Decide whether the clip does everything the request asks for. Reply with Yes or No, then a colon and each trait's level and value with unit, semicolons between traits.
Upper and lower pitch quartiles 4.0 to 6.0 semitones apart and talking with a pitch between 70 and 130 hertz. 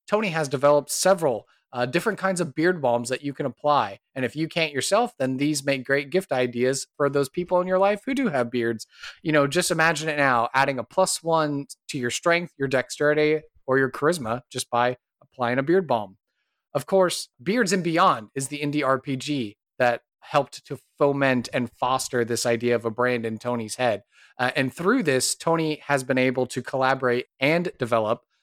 No: average, 4.5 semitones; medium, 140 Hz